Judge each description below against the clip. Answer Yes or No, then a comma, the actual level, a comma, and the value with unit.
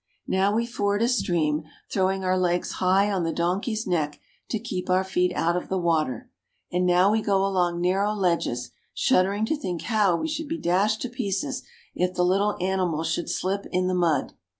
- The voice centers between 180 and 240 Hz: Yes, medium, 185 Hz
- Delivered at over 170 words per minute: Yes, average, 195 wpm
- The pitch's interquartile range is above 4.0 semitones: No, average, 2.8 semitones